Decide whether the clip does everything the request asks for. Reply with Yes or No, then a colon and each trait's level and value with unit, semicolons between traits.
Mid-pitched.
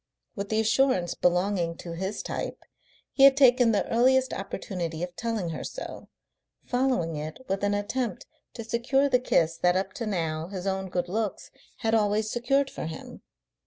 No: high, 205 Hz